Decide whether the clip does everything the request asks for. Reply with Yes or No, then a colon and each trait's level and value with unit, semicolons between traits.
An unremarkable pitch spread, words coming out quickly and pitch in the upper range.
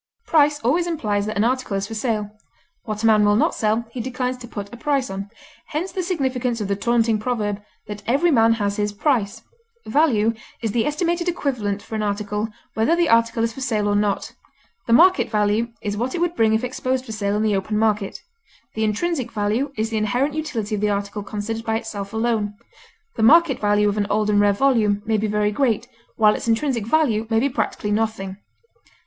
Yes: average, 3.5 semitones; fast, 210 wpm; high, 225 Hz